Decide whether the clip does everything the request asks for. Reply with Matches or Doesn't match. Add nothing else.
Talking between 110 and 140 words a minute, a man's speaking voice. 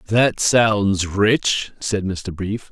Matches